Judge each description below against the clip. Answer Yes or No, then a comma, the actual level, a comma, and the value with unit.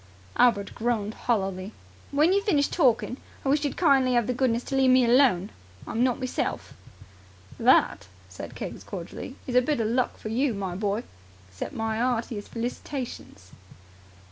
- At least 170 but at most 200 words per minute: No, average, 160 wpm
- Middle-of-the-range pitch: No, high, 245 Hz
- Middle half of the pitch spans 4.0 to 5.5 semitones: No, average, 3.4 semitones